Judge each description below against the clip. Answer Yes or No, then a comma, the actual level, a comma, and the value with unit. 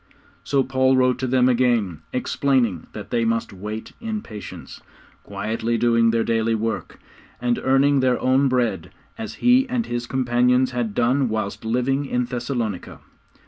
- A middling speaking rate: Yes, average, 150 wpm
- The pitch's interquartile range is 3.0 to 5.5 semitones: No, narrow, 2.5 semitones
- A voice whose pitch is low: Yes, low, 120 Hz